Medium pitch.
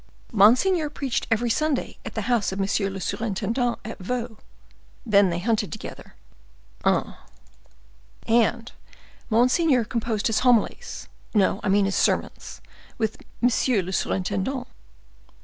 No: high, 225 Hz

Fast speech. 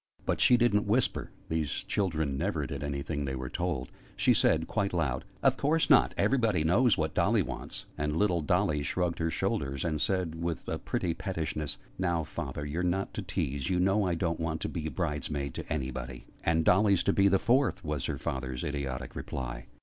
No: average, 195 wpm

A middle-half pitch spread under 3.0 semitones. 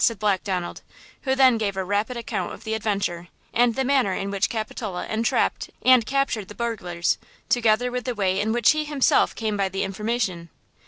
No: average, 3.8 semitones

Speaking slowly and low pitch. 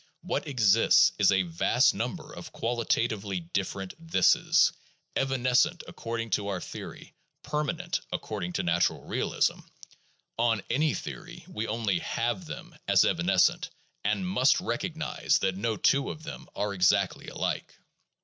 Yes: slow, 130 wpm; low, 115 Hz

